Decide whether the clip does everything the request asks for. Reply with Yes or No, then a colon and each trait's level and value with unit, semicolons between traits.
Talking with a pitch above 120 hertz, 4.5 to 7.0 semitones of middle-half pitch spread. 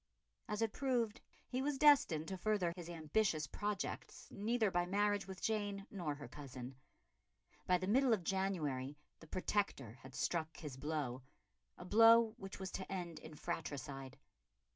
Yes: medium, 185 Hz; wide, 5.5 semitones